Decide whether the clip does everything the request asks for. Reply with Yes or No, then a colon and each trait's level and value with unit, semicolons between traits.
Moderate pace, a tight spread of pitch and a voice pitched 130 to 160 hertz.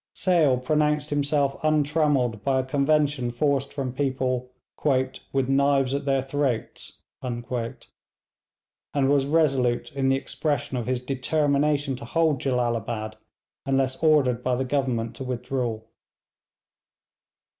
No: slow, 115 wpm; narrow, 2.3 semitones; low, 135 Hz